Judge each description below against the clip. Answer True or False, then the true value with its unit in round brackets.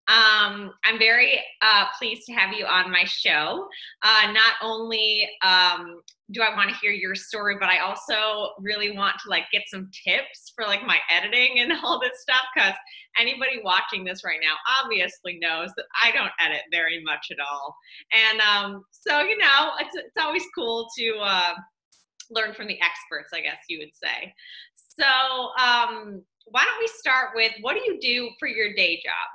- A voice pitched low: False (215 Hz)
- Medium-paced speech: True (185 wpm)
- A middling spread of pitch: True (4.9 semitones)